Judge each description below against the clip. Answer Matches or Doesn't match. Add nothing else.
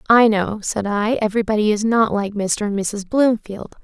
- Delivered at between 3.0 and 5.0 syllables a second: Matches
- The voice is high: Matches